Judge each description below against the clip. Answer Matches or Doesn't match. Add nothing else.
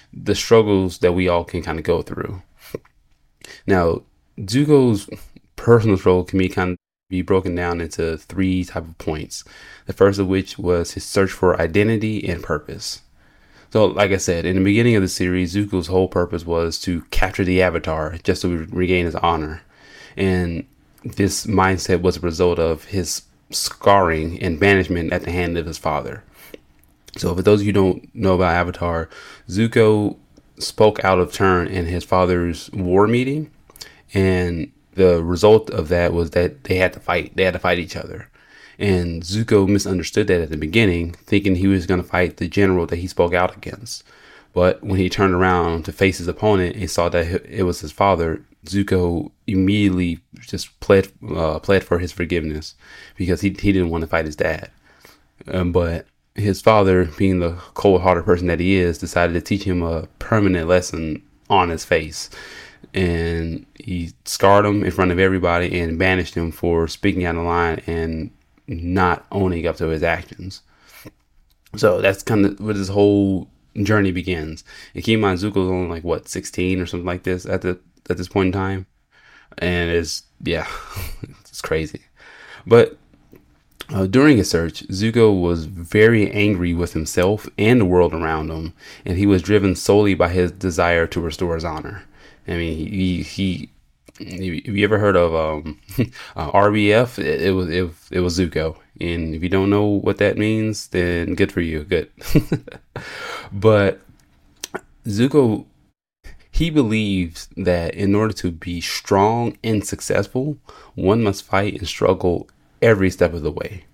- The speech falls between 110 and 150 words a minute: Doesn't match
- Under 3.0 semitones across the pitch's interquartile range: Matches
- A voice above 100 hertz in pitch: Doesn't match